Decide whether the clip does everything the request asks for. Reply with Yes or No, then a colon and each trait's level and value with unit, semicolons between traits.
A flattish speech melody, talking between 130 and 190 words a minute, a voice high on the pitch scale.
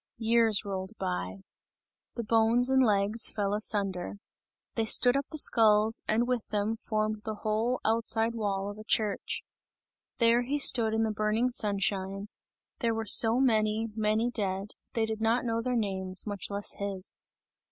Yes: narrow, 2.2 semitones; average, 160 wpm; high, 220 Hz